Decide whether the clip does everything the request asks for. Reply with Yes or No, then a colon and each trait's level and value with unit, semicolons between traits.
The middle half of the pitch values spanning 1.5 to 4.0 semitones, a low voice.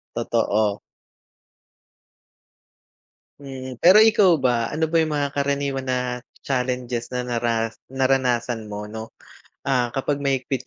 Yes: average, 2.9 semitones; low, 130 Hz